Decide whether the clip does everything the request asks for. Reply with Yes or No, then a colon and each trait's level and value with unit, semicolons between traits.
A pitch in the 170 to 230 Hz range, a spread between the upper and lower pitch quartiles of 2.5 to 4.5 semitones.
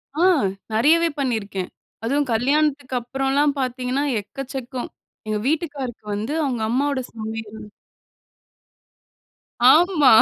No: very high, 265 Hz; average, 4.2 semitones